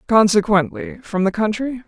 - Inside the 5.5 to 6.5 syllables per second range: No, 4.9 syllables/s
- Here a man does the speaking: No, female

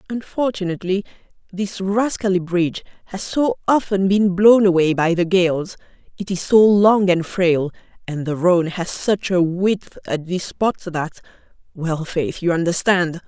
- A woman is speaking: Yes, female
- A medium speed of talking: Yes, average, 150 wpm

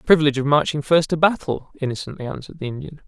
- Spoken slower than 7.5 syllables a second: No, 7.6 syllables/s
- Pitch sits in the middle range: Yes, medium, 145 Hz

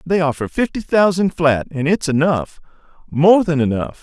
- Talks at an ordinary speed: Yes, average, 150 wpm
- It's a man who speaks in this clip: Yes, male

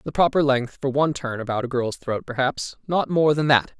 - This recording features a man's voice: Yes, male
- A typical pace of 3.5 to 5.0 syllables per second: No, 5.4 syllables/s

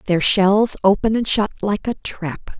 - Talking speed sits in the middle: Yes, average, 185 wpm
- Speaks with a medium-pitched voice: No, high, 200 Hz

